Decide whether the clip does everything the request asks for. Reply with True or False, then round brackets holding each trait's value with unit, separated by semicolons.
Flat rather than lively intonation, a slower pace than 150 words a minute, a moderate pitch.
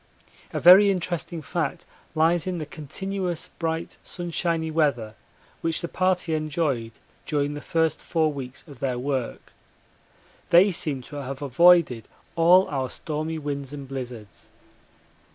False (3.7 semitones; 135 wpm; 155 Hz)